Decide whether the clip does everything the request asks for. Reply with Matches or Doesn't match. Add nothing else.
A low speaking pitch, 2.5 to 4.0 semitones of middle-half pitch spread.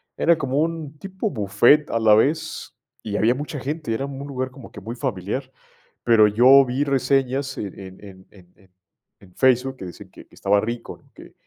Doesn't match